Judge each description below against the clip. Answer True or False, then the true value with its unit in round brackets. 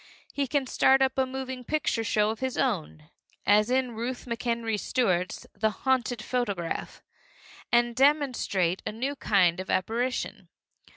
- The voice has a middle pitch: False (240 Hz)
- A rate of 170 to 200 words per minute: False (140 wpm)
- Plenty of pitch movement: False (3.9 semitones)